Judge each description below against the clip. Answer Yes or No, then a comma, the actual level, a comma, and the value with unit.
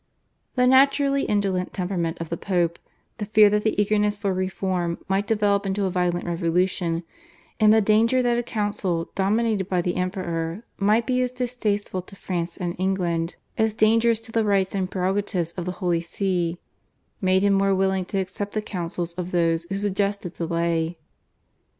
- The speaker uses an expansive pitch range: No, average, 3.0 semitones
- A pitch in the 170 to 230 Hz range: Yes, high, 190 Hz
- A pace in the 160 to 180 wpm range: Yes, average, 170 wpm